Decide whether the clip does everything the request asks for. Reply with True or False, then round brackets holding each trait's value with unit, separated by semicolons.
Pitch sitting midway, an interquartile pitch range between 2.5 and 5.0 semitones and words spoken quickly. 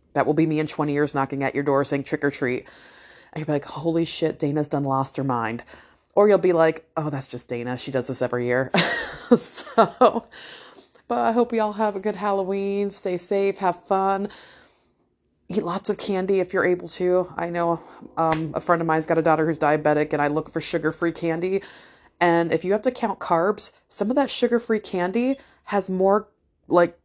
True (170 Hz; 4.7 semitones; 210 wpm)